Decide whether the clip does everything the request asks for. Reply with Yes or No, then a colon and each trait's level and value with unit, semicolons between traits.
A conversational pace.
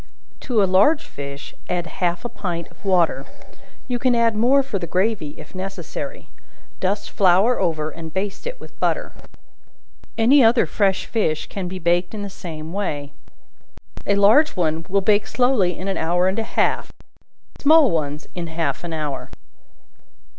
Yes: average, 165 wpm